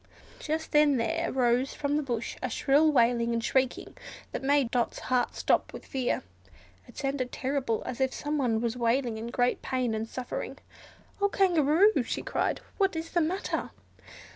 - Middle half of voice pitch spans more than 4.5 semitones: No, average, 3.8 semitones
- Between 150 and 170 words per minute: Yes, average, 165 wpm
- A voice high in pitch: Yes, very high, 260 Hz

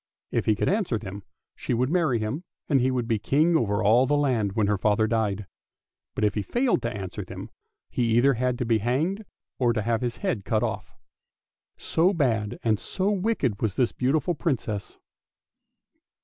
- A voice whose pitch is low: Yes, low, 120 Hz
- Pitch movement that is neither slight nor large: Yes, average, 5.0 semitones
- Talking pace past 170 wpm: Yes, average, 190 wpm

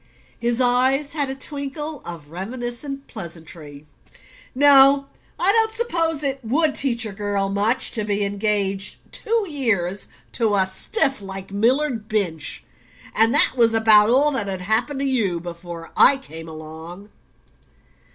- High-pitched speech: Yes, high, 225 Hz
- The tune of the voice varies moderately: No, wide, 6.0 semitones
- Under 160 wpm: Yes, average, 140 wpm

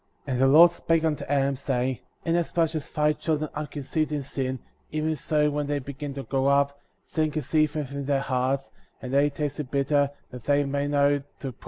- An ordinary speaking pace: No, fast, 215 wpm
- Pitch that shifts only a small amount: Yes, narrow, 1.8 semitones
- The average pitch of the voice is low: No, medium, 145 Hz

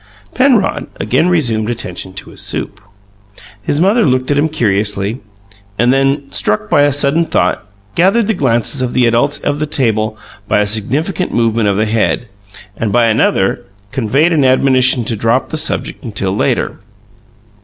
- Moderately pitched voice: No, low, 125 Hz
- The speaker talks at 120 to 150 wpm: No, average, 165 wpm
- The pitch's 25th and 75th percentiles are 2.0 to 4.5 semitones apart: No, average, 5.1 semitones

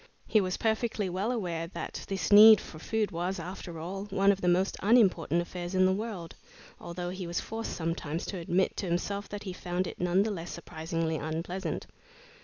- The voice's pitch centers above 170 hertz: Yes, medium, 185 Hz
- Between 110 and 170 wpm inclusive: No, average, 195 wpm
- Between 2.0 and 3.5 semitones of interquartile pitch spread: Yes, average, 2.8 semitones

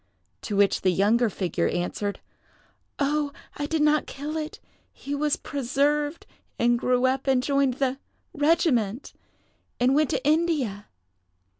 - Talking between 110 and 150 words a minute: Yes, average, 140 wpm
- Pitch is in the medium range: No, very high, 275 Hz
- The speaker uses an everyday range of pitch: Yes, average, 3.9 semitones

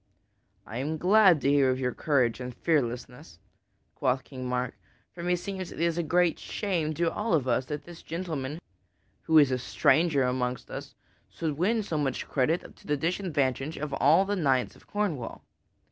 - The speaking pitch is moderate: Yes, medium, 150 Hz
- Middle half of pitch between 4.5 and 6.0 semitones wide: Yes, average, 4.8 semitones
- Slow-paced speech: No, average, 175 wpm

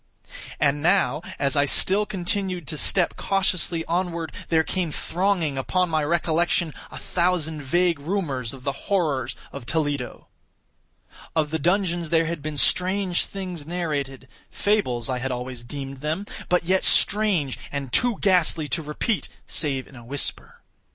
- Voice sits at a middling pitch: Yes, medium, 160 Hz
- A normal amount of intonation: Yes, average, 4.4 semitones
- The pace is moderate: Yes, average, 145 wpm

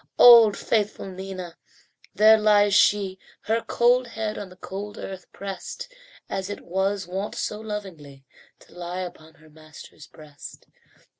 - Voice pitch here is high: Yes, high, 195 Hz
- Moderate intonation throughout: Yes, average, 3.0 semitones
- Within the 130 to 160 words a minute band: Yes, average, 140 wpm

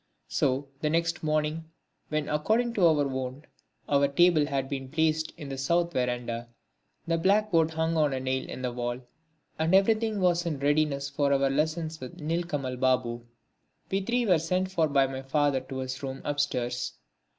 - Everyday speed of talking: Yes, average, 175 wpm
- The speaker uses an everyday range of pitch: Yes, average, 3.8 semitones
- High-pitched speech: No, medium, 150 Hz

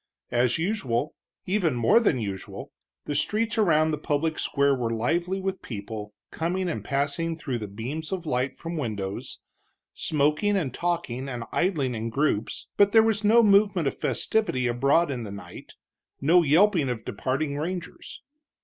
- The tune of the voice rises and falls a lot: Yes, wide, 6.6 semitones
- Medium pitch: Yes, medium, 150 Hz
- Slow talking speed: No, average, 160 wpm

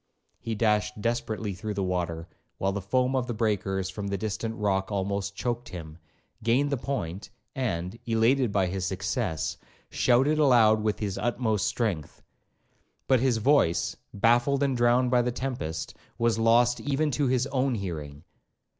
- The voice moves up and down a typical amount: Yes, average, 4.2 semitones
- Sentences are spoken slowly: No, average, 155 wpm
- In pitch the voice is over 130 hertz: No, low, 110 Hz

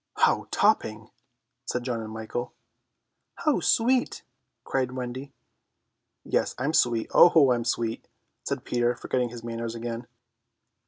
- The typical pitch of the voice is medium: No, low, 120 Hz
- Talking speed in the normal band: No, slow, 125 wpm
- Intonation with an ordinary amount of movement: No, narrow, 1.9 semitones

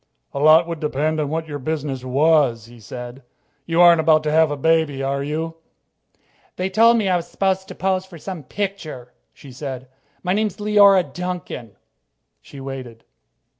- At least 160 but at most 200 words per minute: Yes, average, 170 wpm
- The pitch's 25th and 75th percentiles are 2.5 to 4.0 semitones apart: No, average, 4.8 semitones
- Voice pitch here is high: No, medium, 155 Hz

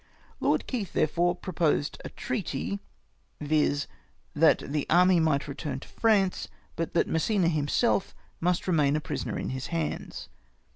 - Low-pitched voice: No, medium, 165 Hz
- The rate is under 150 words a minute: Yes, average, 140 wpm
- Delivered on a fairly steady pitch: No, average, 3.6 semitones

